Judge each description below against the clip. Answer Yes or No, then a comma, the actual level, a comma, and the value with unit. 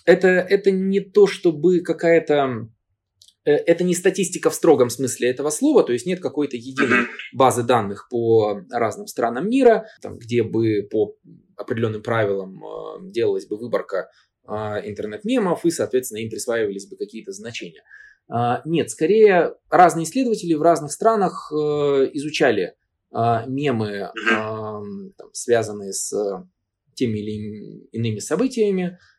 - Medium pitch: Yes, medium, 145 Hz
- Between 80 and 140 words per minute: Yes, average, 115 wpm